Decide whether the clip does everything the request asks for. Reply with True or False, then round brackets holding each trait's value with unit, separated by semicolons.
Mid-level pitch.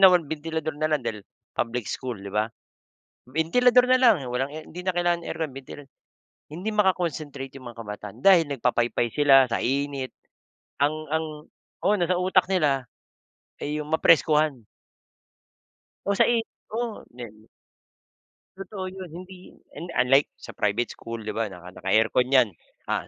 True (150 Hz)